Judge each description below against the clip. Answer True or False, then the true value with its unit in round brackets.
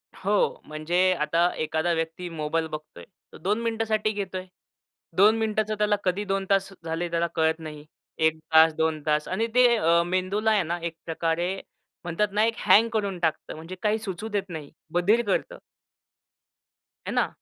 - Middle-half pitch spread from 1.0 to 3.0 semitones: False (4.5 semitones)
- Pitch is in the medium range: True (180 Hz)